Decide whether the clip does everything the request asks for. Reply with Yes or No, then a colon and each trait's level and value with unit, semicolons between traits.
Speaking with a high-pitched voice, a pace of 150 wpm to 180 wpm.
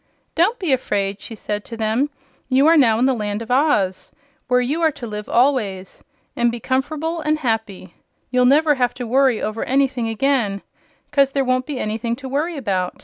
No: very high, 250 Hz; average, 195 wpm